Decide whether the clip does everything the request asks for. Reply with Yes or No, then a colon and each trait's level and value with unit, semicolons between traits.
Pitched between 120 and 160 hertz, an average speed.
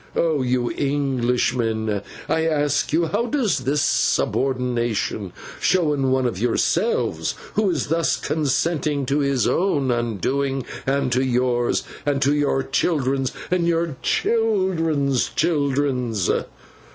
No: medium, 140 Hz; slow, 120 wpm